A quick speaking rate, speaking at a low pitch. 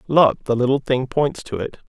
Yes: fast, 220 wpm; low, 130 Hz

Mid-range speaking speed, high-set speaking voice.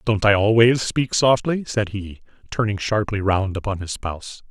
No: average, 175 wpm; low, 105 Hz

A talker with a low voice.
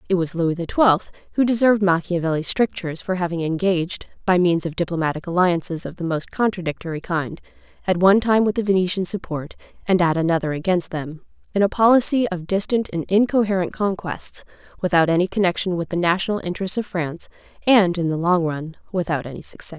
No: medium, 180 Hz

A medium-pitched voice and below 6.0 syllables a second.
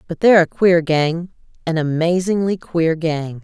Yes: medium, 170 Hz; 4.4 syllables/s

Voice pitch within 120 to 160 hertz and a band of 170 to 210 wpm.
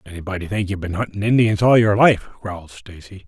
No: low, 100 Hz; average, 200 wpm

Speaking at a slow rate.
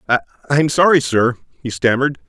Yes: slow, 130 wpm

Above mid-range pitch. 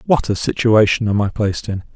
No: low, 110 Hz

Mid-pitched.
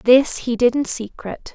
No: high, 245 Hz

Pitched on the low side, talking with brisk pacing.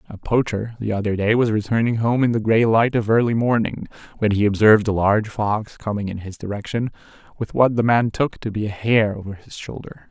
Yes: low, 110 Hz; fast, 220 wpm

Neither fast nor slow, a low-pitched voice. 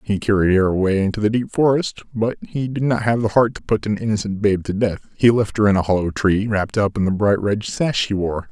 No: fast, 270 wpm; low, 105 Hz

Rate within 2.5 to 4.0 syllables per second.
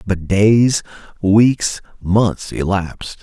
Yes: 2.8 syllables/s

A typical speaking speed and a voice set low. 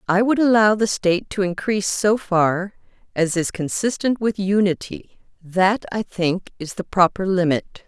No: average, 160 wpm; high, 195 Hz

